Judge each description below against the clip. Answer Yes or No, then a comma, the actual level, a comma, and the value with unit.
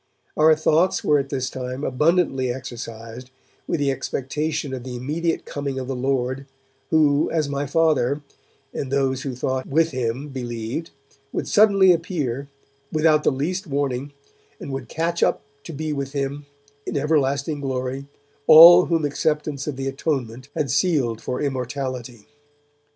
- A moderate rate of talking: Yes, average, 150 wpm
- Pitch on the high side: No, medium, 140 Hz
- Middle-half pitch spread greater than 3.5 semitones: No, average, 3.0 semitones